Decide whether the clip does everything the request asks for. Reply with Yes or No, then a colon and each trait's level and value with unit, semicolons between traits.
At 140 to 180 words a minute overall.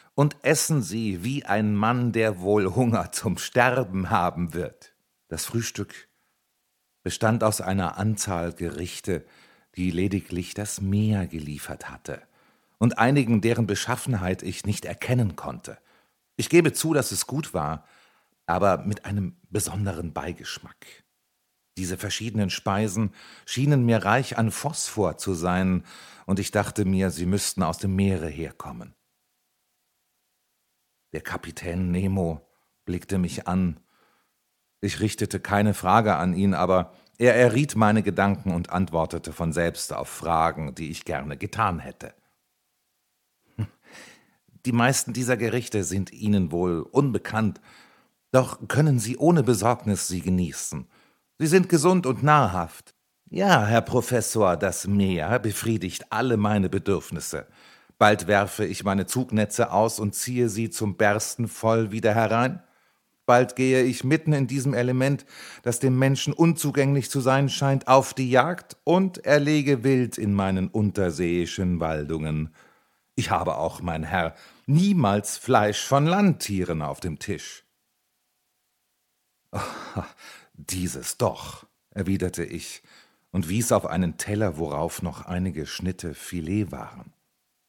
No: average, 130 wpm